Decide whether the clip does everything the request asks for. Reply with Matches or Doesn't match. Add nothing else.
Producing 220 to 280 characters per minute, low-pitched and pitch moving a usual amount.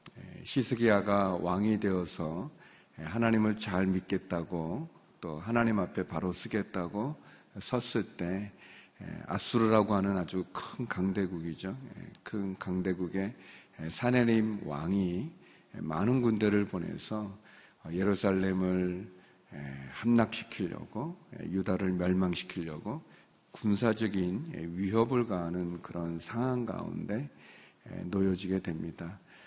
Matches